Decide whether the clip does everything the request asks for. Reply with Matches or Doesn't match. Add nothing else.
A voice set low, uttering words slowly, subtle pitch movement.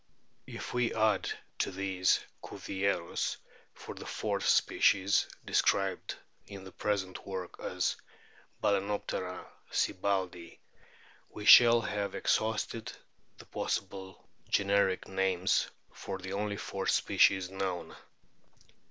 Matches